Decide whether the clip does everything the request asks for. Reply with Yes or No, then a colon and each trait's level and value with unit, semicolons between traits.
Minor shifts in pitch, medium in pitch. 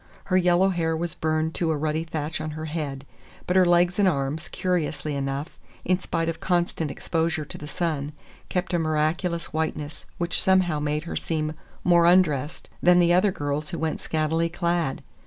Yes: narrow, 2.3 semitones; medium, 160 Hz